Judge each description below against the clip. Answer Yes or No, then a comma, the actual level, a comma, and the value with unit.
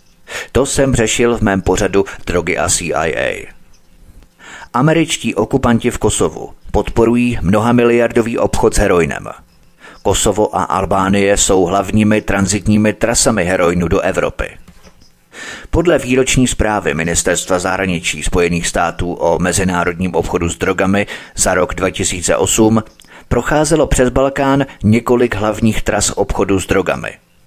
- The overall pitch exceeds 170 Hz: No, low, 105 Hz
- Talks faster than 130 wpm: No, slow, 115 wpm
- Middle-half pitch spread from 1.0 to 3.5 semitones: No, average, 4.0 semitones